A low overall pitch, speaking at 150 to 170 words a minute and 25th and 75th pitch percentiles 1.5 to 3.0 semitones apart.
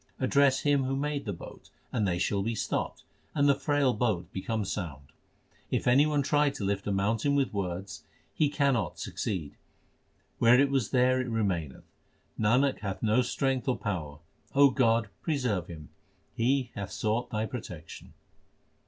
No: low, 115 Hz; average, 160 wpm; wide, 5.5 semitones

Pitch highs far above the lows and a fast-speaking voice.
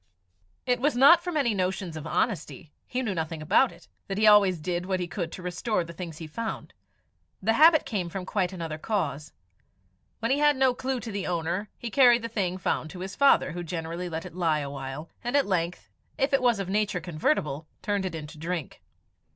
Yes: wide, 5.9 semitones; fast, 215 wpm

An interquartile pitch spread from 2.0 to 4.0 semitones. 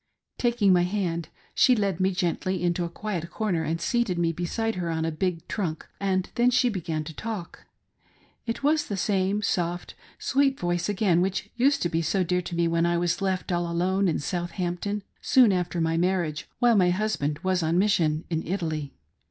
Yes: average, 3.2 semitones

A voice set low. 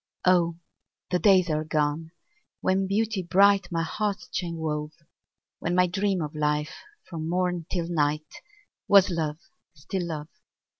No: medium, 170 Hz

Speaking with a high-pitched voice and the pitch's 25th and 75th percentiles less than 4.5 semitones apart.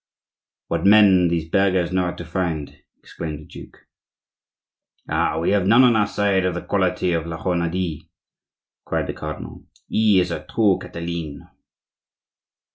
No: very low, 90 Hz; average, 2.8 semitones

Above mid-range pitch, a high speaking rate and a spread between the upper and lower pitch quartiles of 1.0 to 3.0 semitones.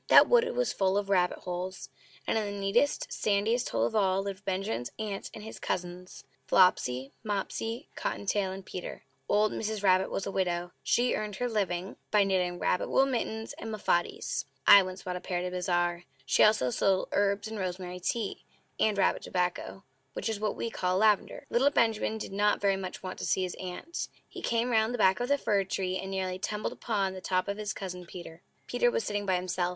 Yes: high, 195 Hz; fast, 210 wpm; average, 2.7 semitones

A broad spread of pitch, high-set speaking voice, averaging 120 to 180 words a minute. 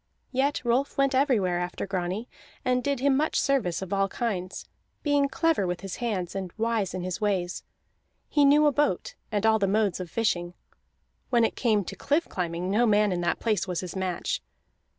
No: wide, 6.0 semitones; high, 210 Hz; average, 190 wpm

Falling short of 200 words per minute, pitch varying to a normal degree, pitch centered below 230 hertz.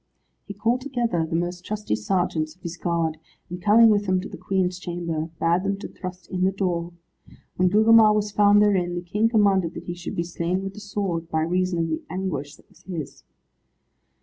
No: fast, 205 wpm; average, 3.1 semitones; medium, 185 Hz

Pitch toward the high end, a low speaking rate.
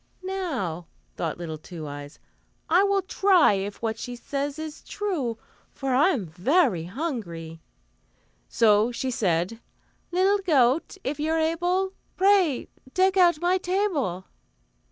Yes: very high, 275 Hz; slow, 130 wpm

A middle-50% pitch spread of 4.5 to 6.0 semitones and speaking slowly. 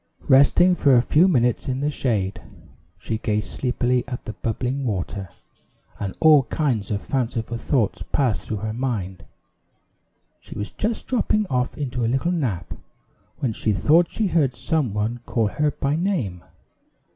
No: wide, 5.4 semitones; average, 155 wpm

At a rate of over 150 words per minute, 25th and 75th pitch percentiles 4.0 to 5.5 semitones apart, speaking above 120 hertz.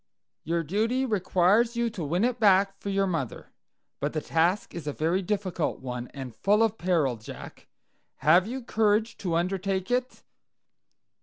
Yes: average, 160 wpm; average, 4.5 semitones; high, 190 Hz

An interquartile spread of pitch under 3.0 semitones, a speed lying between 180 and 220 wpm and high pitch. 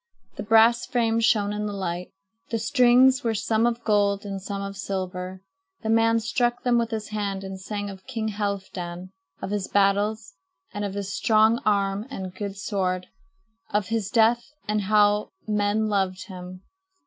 No: narrow, 2.4 semitones; average, 170 wpm; high, 205 Hz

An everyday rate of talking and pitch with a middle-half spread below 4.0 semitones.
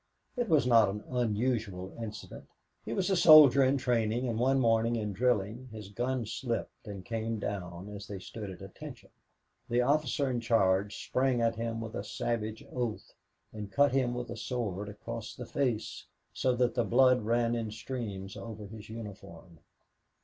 Yes: average, 170 wpm; average, 3.0 semitones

